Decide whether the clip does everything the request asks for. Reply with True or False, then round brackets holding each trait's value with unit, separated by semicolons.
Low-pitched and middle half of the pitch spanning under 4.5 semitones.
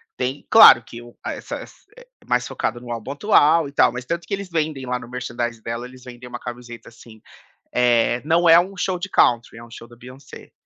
False (125 Hz; 5.1 semitones)